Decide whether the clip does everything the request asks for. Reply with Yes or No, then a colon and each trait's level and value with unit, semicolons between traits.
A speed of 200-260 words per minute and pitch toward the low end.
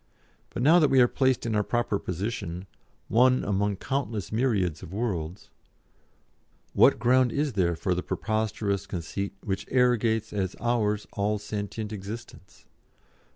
No: average, 140 wpm; low, 105 Hz